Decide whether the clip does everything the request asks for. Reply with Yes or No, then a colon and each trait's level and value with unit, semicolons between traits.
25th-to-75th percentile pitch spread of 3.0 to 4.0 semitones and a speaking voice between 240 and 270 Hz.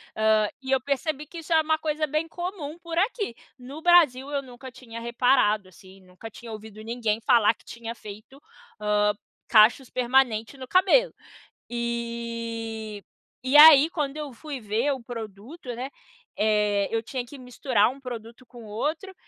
No: average, 4.8 semitones; high, 245 Hz